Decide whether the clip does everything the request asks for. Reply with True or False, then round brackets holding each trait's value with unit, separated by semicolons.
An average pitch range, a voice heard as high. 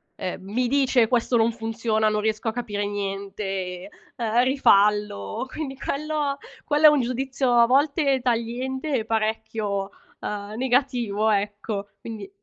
True (4.1 semitones; 225 Hz)